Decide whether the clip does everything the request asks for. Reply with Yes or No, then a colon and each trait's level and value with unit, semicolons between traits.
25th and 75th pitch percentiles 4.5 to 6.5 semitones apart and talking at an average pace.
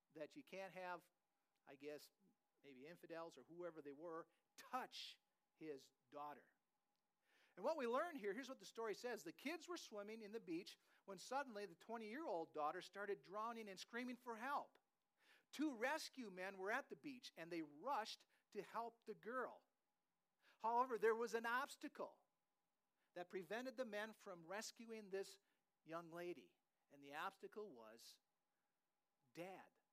Yes: wide, 5.5 semitones; average, 155 wpm